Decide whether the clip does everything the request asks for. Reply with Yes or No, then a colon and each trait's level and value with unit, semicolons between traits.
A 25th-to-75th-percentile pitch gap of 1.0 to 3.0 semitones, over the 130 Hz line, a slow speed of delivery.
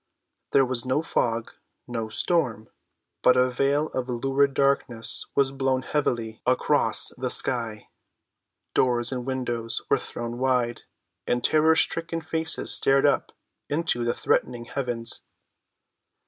No: narrow, 2.6 semitones; low, 125 Hz; slow, 120 wpm